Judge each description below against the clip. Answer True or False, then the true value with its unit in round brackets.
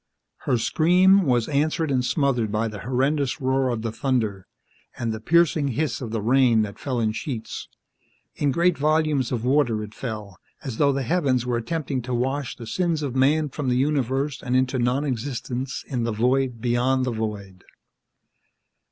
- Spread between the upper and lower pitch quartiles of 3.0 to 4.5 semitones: True (3.7 semitones)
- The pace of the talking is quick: False (180 wpm)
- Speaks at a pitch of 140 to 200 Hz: False (130 Hz)